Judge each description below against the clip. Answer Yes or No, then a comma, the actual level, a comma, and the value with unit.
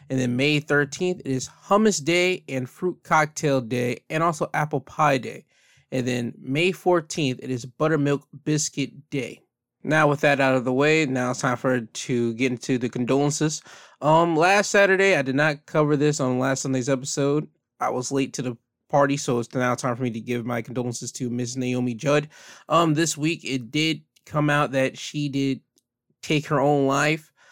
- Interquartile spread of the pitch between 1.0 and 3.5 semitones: Yes, average, 3.2 semitones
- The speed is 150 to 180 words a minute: No, average, 190 wpm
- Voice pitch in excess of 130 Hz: Yes, medium, 140 Hz